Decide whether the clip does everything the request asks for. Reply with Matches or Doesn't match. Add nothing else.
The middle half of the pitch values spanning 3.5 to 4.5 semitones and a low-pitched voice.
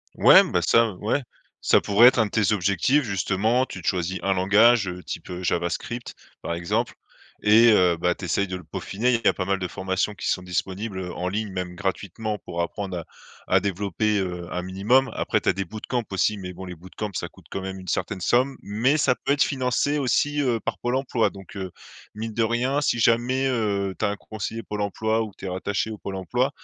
Matches